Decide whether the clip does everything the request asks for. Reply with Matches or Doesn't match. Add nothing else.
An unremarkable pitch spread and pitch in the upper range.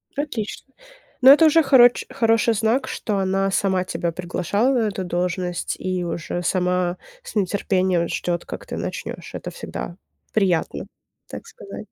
Matches